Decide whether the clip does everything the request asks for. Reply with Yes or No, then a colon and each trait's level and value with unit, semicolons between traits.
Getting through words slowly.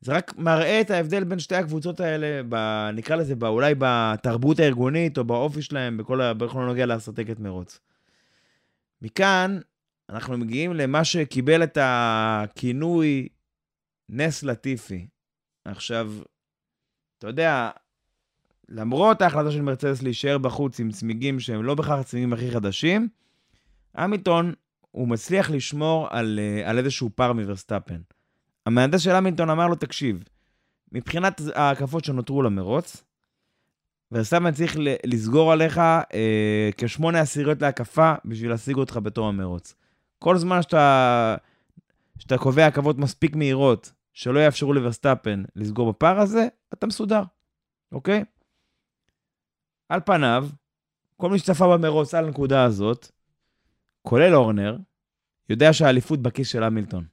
No: average, 120 wpm